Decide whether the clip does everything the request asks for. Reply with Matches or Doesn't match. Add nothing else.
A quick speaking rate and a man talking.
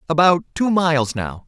Doesn't match